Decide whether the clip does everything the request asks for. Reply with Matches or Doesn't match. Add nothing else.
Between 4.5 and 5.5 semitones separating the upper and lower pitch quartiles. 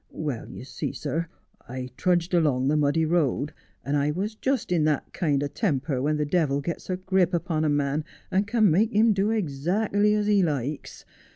Matches